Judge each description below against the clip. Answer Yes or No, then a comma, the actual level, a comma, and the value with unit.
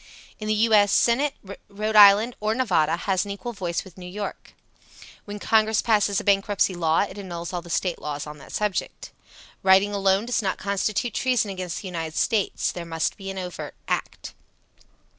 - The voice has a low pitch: No, high, 200 Hz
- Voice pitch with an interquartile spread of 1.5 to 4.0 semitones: Yes, average, 3.0 semitones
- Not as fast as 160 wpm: No, average, 185 wpm